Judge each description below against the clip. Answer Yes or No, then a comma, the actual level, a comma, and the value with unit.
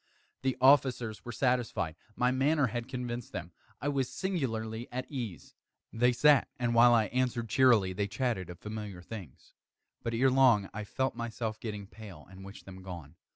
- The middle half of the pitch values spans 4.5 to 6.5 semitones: No, average, 3.8 semitones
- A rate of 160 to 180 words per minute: Yes, average, 170 wpm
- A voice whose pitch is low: Yes, low, 115 Hz